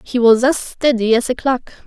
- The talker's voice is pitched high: Yes, high, 245 Hz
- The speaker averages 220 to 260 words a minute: Yes, fast, 225 wpm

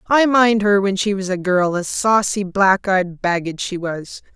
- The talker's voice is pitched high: Yes, high, 195 Hz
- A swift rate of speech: No, average, 195 wpm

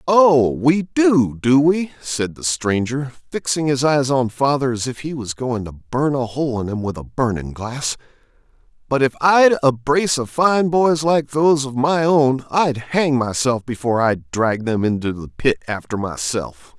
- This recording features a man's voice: Yes, male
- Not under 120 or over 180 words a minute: No, average, 190 wpm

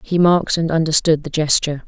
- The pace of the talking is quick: No, average, 195 wpm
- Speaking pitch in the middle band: Yes, medium, 160 Hz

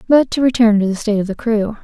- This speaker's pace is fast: Yes, fast, 295 wpm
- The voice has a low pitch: No, high, 220 Hz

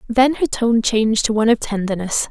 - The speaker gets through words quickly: Yes, fast, 210 wpm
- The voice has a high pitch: Yes, high, 225 Hz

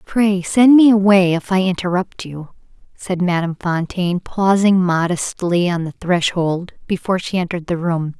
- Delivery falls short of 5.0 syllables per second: Yes, 4.8 syllables/s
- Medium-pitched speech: Yes, medium, 180 Hz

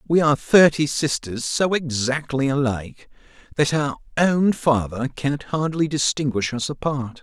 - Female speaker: No, male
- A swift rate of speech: No, slow, 135 wpm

